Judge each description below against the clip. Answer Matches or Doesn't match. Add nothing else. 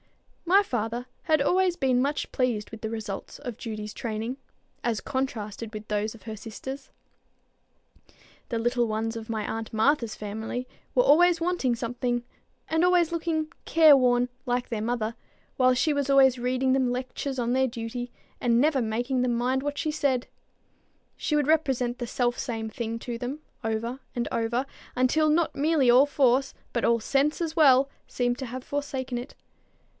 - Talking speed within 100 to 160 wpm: Doesn't match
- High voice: Matches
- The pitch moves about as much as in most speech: Matches